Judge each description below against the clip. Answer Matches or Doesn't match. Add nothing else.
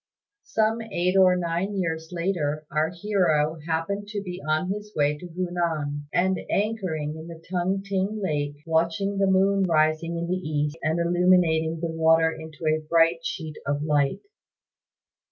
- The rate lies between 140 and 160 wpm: Matches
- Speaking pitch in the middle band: Matches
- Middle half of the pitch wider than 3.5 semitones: Doesn't match